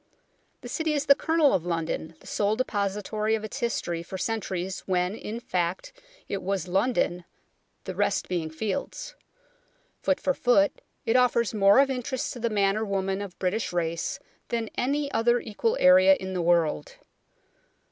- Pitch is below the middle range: No, high, 205 Hz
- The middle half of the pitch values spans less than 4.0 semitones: No, average, 4.7 semitones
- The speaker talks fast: No, average, 165 wpm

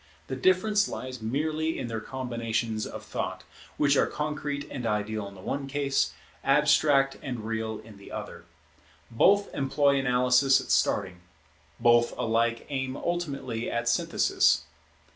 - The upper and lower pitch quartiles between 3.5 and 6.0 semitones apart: Yes, average, 3.9 semitones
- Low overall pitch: Yes, low, 125 Hz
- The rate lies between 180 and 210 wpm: No, average, 140 wpm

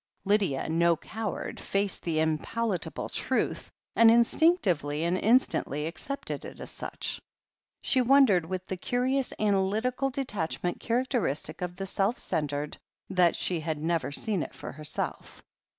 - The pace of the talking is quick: No, slow, 135 wpm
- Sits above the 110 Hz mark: Yes, high, 190 Hz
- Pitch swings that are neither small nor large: No, wide, 6.2 semitones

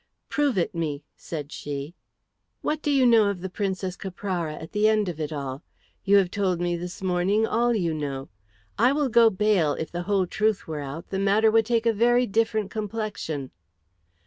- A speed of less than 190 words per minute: No, average, 195 wpm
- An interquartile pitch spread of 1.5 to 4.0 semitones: No, average, 4.7 semitones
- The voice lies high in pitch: Yes, high, 195 Hz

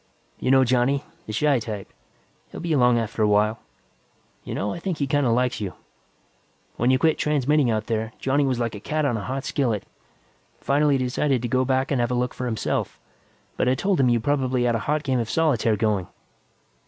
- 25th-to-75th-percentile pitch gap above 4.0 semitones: No, average, 3.5 semitones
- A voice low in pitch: Yes, low, 125 Hz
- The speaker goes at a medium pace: No, fast, 210 wpm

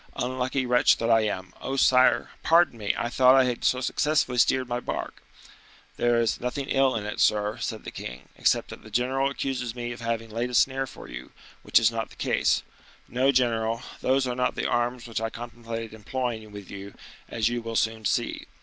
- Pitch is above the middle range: No, low, 120 Hz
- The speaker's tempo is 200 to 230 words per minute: Yes, fast, 205 wpm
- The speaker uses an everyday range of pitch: No, narrow, 2.2 semitones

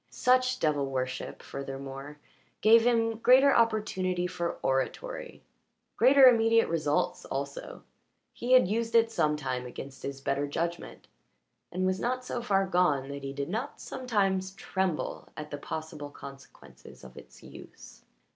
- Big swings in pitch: Yes, wide, 8.4 semitones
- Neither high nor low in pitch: Yes, medium, 180 Hz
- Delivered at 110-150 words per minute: Yes, slow, 135 wpm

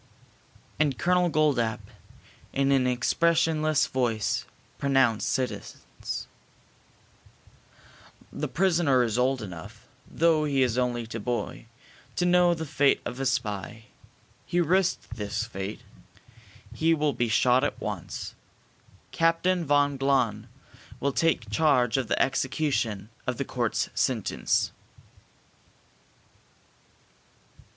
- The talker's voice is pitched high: No, low, 135 Hz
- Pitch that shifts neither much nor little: Yes, average, 4.8 semitones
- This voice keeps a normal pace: No, slow, 110 wpm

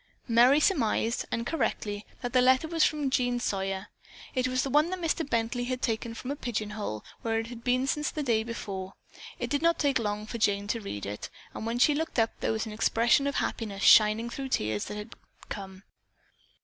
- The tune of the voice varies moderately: Yes, average, 3.9 semitones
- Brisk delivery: Yes, fast, 215 wpm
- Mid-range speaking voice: No, high, 235 Hz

